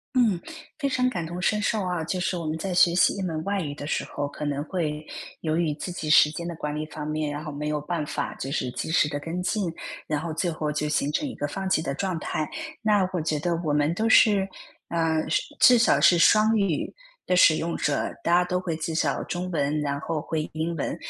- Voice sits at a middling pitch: Yes, medium, 165 Hz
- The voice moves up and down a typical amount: Yes, average, 3.3 semitones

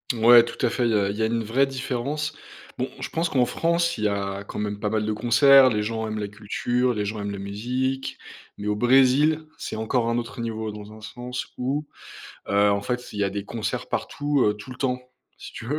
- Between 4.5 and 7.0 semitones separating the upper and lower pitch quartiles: No, average, 3.7 semitones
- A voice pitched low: Yes, low, 115 Hz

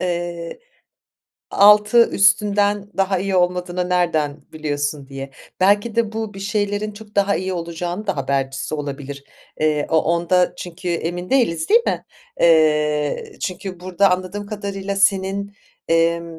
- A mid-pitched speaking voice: Yes, medium, 180 Hz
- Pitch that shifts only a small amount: No, average, 3.8 semitones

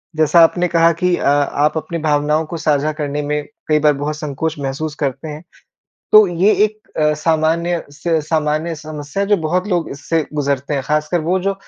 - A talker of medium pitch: Yes, medium, 155 Hz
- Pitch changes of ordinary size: No, narrow, 2.2 semitones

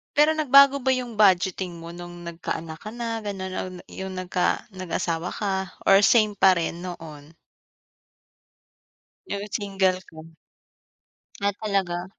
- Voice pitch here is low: No, high, 190 Hz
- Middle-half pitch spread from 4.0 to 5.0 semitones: No, average, 3.3 semitones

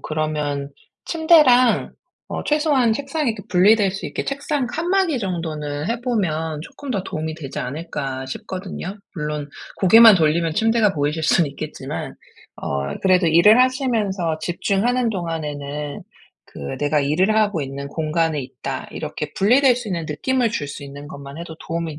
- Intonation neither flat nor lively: No, wide, 7.3 semitones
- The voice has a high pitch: No, medium, 170 Hz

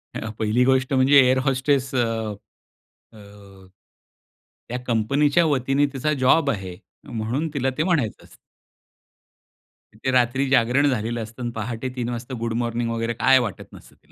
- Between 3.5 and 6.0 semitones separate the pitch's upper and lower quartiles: No, average, 2.9 semitones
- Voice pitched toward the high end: No, low, 125 Hz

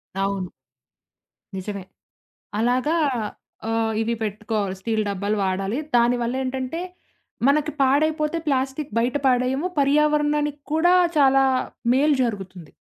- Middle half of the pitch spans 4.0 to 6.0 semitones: Yes, wide, 5.5 semitones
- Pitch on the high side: Yes, very high, 250 Hz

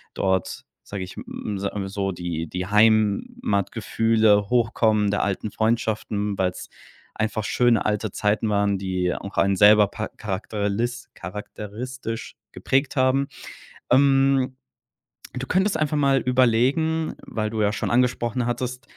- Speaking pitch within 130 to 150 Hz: No, low, 110 Hz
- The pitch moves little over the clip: No, average, 3.8 semitones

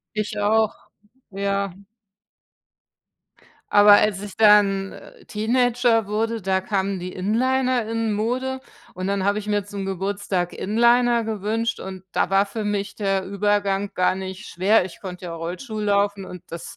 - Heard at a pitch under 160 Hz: No, high, 205 Hz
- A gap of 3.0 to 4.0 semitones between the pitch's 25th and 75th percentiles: No, narrow, 2.4 semitones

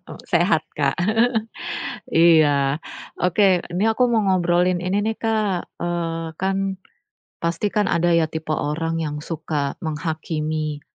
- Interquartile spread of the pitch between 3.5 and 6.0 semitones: No, average, 2.7 semitones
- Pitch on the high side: No, medium, 170 Hz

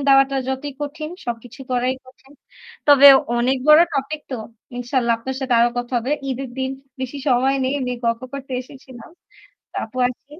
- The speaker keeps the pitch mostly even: Yes, narrow, 1.9 semitones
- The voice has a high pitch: Yes, very high, 260 Hz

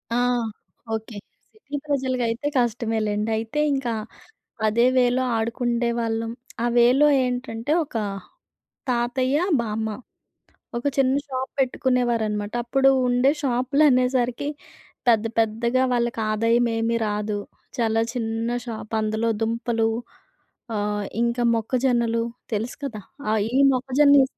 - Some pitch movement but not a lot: No, narrow, 2.3 semitones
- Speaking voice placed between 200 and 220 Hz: No, high, 235 Hz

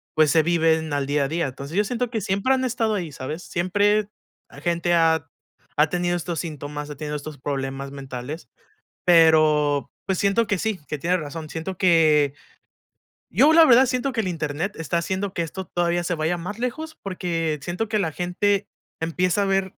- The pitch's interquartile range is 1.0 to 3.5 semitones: No, average, 4.4 semitones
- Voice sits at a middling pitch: Yes, medium, 170 Hz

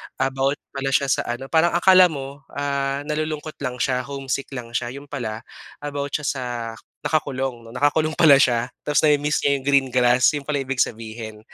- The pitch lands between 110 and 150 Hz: Yes, medium, 140 Hz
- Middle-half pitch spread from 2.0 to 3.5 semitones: Yes, narrow, 2.5 semitones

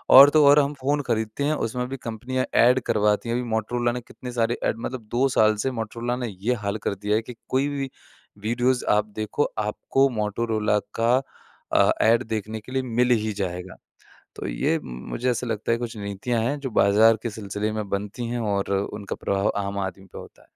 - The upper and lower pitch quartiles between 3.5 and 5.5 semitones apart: No, average, 3.0 semitones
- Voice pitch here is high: No, low, 115 Hz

